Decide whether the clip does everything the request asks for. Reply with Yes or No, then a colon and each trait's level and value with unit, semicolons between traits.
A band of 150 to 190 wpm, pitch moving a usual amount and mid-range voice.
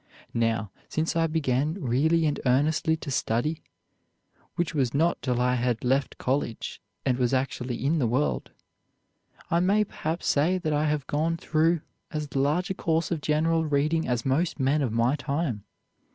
Yes: average, 165 wpm; average, 4.1 semitones; medium, 150 Hz